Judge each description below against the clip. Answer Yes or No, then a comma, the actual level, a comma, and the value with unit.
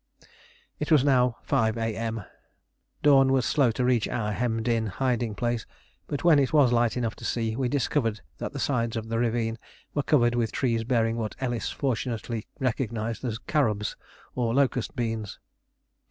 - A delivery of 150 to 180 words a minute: Yes, average, 170 wpm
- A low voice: Yes, low, 120 Hz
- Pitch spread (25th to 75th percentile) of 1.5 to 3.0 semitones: Yes, narrow, 2.5 semitones